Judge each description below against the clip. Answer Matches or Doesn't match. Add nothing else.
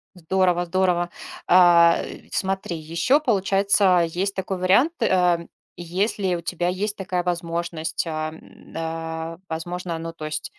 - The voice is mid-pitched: Matches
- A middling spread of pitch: Doesn't match